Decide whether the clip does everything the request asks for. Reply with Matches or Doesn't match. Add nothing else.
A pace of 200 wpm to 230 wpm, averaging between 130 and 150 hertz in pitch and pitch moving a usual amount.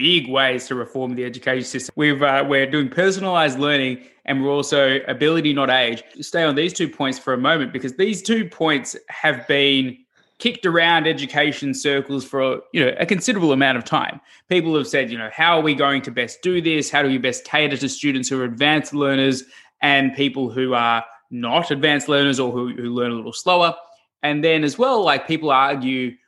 Matches